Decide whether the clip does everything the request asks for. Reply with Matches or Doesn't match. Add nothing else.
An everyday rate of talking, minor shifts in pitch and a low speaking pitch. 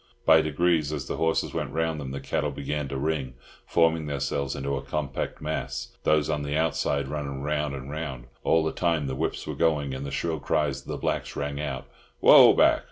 Doesn't match